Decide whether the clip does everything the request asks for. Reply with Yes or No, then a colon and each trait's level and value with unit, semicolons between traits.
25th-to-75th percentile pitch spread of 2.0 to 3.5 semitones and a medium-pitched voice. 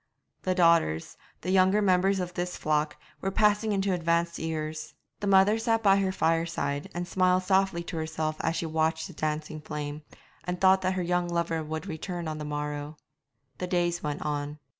Yes: average, 3.2 semitones; medium, 170 Hz